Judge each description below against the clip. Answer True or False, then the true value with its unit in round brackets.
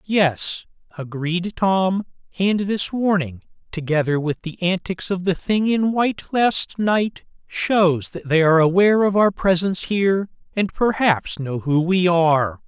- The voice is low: False (180 Hz)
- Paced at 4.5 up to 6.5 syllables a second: False (4.2 syllables/s)